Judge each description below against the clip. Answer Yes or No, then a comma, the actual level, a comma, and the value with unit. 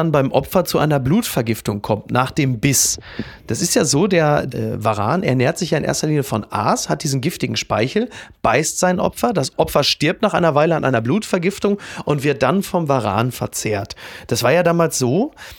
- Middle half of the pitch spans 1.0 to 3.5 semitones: No, wide, 5.4 semitones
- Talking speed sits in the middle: No, fast, 200 wpm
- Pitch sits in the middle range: Yes, medium, 145 Hz